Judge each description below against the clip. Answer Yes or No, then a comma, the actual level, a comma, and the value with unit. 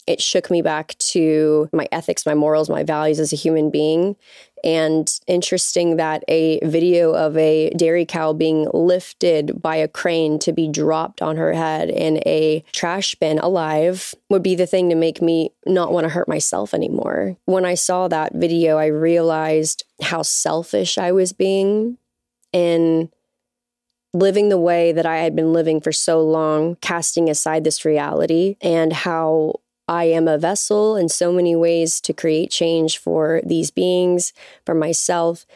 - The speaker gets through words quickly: No, average, 165 wpm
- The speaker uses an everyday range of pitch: No, narrow, 2.1 semitones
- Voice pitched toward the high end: No, medium, 165 Hz